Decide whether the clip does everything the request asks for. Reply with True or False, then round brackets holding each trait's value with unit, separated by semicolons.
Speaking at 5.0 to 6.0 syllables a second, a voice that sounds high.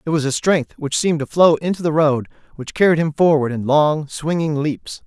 False (5.2 syllables/s; 155 Hz)